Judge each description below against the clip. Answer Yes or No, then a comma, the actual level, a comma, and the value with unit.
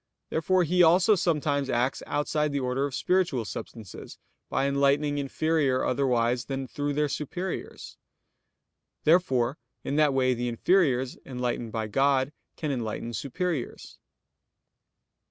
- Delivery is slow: Yes, slow, 120 wpm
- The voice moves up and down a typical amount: Yes, average, 3.5 semitones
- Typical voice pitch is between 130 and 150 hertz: Yes, medium, 140 Hz